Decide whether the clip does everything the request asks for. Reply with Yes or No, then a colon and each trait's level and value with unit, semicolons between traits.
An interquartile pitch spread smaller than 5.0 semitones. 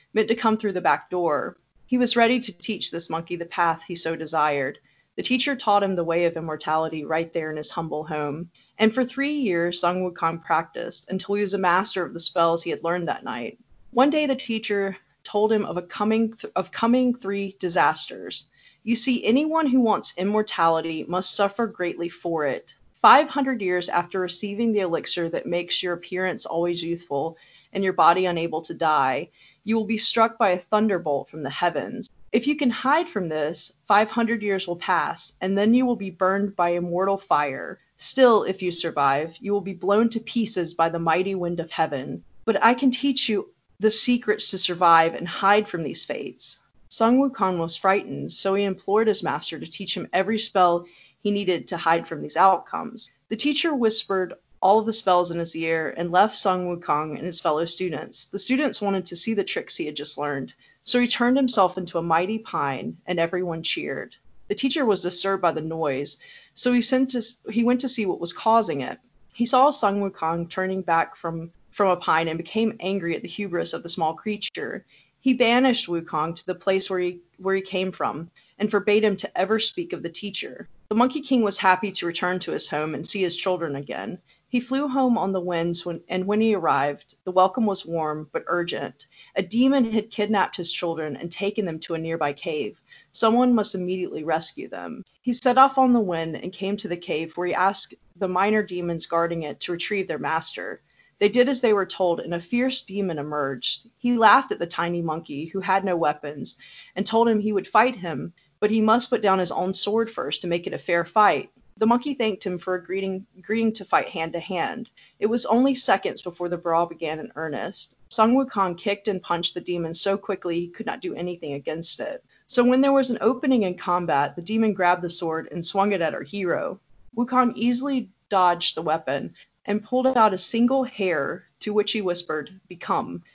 Yes: average, 4.6 semitones